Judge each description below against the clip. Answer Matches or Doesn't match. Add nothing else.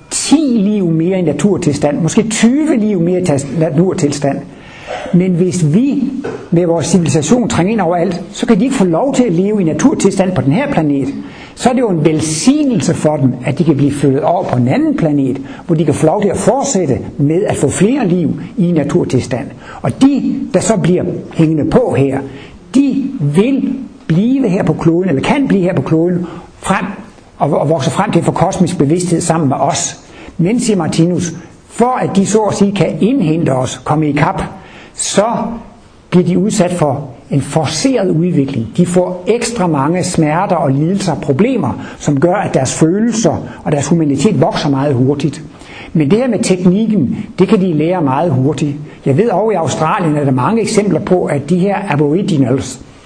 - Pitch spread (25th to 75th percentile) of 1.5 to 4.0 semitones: Doesn't match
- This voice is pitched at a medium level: Matches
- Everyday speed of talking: Matches